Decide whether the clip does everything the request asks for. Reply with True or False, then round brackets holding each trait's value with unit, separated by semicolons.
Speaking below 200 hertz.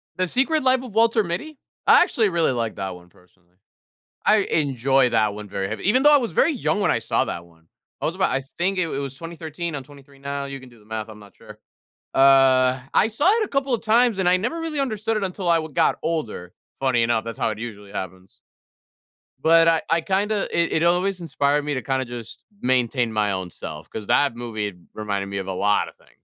True (140 Hz)